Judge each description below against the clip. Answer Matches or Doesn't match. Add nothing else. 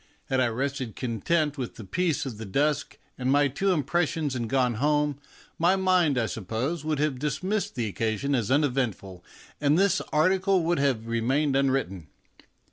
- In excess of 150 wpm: Matches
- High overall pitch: Doesn't match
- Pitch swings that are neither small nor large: Matches